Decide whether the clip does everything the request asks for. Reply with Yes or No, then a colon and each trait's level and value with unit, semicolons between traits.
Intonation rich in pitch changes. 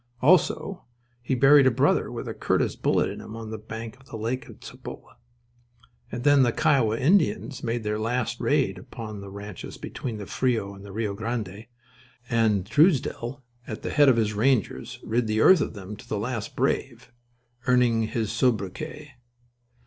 No: average, 3.5 semitones